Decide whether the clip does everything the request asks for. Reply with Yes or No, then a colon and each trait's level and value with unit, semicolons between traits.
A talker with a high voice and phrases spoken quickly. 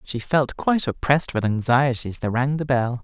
No: low, 130 Hz; fast, 215 wpm